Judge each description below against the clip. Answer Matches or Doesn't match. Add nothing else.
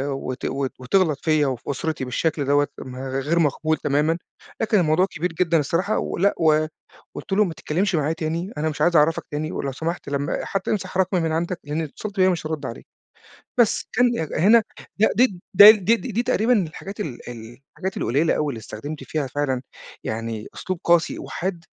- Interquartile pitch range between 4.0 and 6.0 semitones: Matches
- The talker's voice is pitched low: Doesn't match